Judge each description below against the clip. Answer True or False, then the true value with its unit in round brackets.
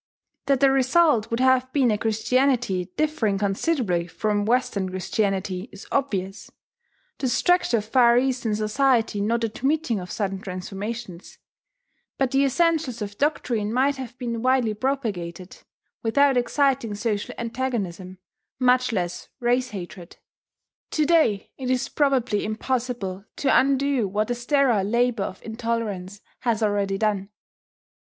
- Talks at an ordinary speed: False (130 wpm)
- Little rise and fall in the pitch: False (4.3 semitones)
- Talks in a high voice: True (230 Hz)